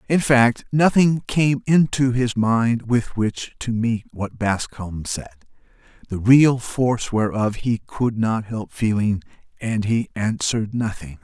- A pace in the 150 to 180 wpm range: No, slow, 135 wpm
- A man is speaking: Yes, male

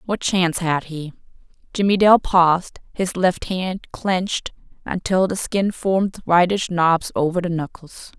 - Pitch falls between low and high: Yes, medium, 180 Hz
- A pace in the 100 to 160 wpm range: Yes, average, 145 wpm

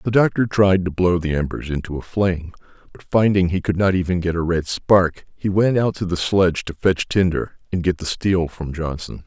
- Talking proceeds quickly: Yes, fast, 225 wpm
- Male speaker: Yes, male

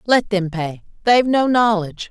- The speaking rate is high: No, average, 145 wpm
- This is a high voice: Yes, high, 205 Hz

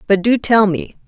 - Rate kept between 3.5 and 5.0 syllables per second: Yes, 4.7 syllables/s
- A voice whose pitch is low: No, high, 205 Hz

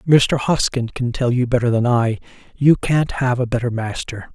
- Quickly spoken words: No, average, 195 wpm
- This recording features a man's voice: Yes, male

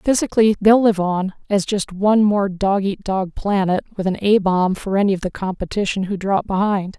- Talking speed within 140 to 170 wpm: No, fast, 205 wpm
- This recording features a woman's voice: Yes, female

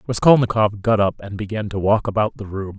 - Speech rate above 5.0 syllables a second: Yes, 5.8 syllables/s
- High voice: No, low, 105 Hz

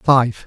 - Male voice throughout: Yes, male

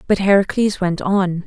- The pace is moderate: Yes, average, 165 wpm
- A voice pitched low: No, high, 190 Hz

